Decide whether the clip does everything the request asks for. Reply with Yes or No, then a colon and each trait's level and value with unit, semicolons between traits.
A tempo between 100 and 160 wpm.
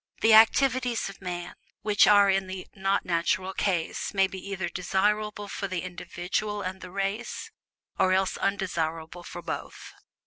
Yes: average, 150 wpm